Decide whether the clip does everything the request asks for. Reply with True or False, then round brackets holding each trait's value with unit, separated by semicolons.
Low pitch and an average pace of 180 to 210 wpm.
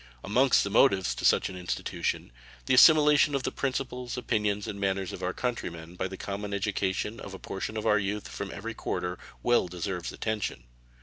True (100 Hz; 190 wpm)